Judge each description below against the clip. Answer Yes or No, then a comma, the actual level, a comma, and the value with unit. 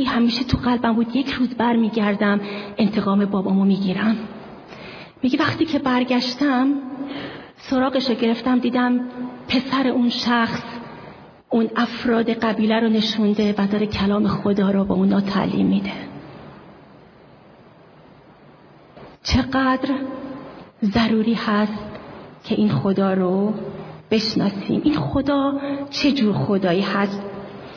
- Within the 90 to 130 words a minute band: Yes, average, 110 wpm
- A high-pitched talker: Yes, high, 225 Hz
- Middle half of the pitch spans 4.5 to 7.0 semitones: No, average, 3.8 semitones